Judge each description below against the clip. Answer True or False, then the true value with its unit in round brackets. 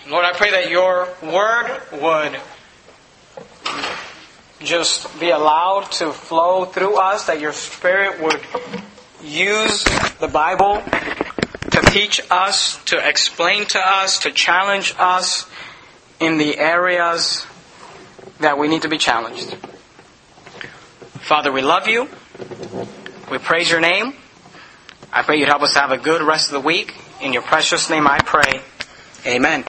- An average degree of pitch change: True (3.7 semitones)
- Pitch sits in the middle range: True (170 Hz)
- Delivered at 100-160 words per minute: True (135 wpm)